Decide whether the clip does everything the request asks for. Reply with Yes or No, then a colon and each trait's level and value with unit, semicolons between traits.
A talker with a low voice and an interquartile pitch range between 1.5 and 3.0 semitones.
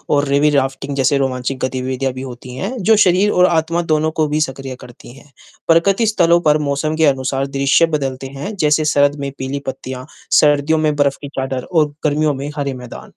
No: medium, 145 Hz; average, 2.7 semitones